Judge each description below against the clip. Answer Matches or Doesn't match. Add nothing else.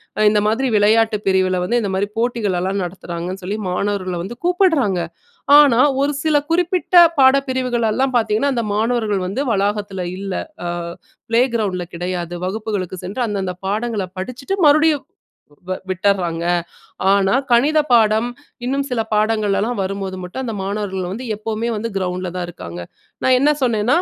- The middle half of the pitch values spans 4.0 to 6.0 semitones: Matches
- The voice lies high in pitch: Matches